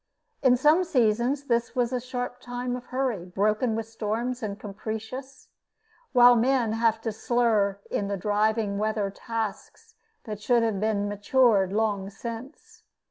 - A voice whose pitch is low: No, high, 225 Hz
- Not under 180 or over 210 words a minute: No, average, 145 wpm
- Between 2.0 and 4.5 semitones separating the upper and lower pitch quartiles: Yes, average, 2.9 semitones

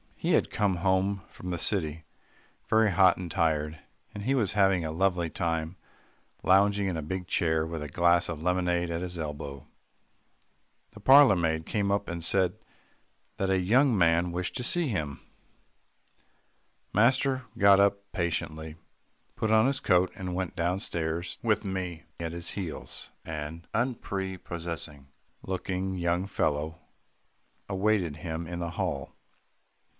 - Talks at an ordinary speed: Yes, average, 145 wpm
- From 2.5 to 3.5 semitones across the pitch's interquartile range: Yes, average, 3.2 semitones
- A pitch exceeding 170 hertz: No, very low, 90 Hz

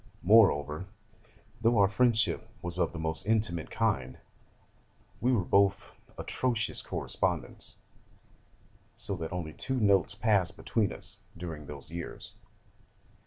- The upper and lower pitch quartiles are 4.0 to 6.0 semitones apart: Yes, average, 5.2 semitones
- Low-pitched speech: Yes, very low, 95 Hz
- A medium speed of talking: No, slow, 120 wpm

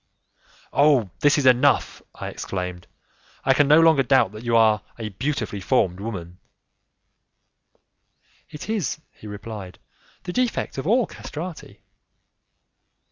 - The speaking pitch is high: No, low, 125 Hz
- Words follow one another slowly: Yes, slow, 125 wpm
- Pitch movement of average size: No, wide, 6.5 semitones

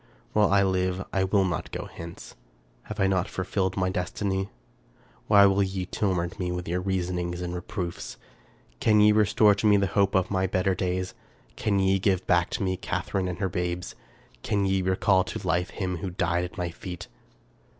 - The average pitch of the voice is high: No, very low, 95 Hz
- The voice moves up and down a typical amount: No, narrow, 1.6 semitones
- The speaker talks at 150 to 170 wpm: No, average, 190 wpm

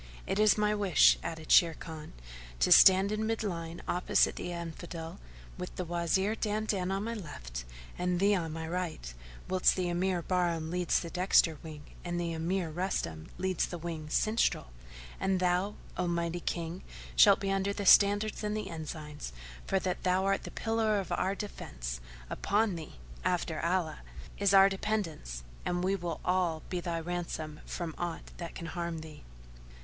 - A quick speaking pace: No, average, 170 wpm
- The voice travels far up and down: No, average, 3.1 semitones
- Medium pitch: Yes, medium, 175 Hz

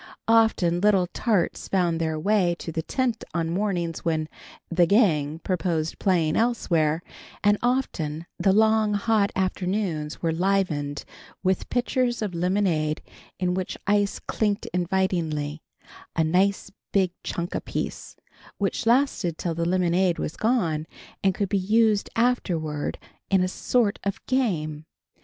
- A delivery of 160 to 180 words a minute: No, slow, 135 wpm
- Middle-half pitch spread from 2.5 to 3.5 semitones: No, average, 4.1 semitones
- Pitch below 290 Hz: Yes, medium, 185 Hz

